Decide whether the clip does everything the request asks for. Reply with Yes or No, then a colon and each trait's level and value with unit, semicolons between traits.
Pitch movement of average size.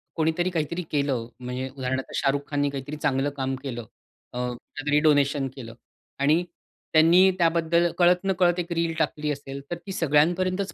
Yes: average, 4.0 semitones